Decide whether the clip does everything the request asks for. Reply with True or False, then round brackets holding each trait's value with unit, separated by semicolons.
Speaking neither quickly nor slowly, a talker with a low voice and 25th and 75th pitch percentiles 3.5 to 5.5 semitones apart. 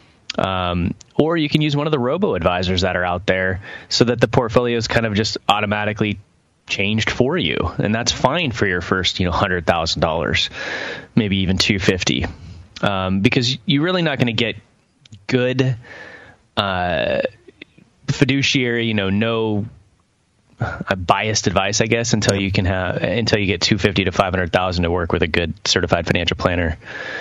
True (180 wpm; 105 Hz; 4.2 semitones)